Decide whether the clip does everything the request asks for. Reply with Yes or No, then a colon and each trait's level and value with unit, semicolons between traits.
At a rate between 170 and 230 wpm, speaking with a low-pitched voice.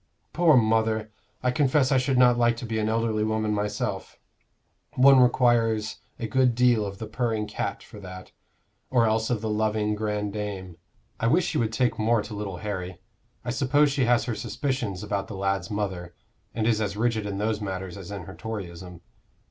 Yes: average, 190 wpm; low, 110 Hz